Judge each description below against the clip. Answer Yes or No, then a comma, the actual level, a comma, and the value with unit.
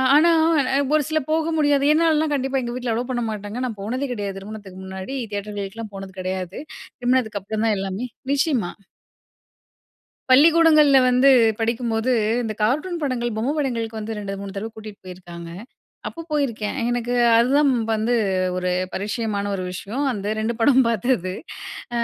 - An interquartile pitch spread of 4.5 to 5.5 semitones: Yes, average, 4.8 semitones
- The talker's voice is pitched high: Yes, high, 230 Hz